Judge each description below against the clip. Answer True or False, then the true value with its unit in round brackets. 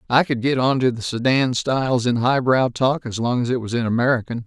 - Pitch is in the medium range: False (125 Hz)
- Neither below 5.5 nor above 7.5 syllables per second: True (5.6 syllables/s)